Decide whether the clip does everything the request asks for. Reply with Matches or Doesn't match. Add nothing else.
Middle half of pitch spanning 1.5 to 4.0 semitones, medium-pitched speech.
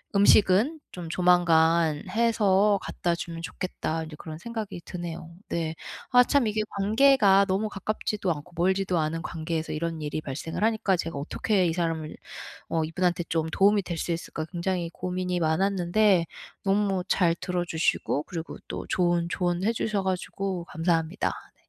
Matches